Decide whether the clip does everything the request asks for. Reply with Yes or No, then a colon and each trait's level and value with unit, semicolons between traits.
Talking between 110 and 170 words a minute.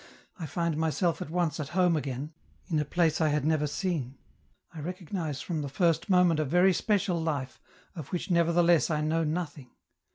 No: average, 185 wpm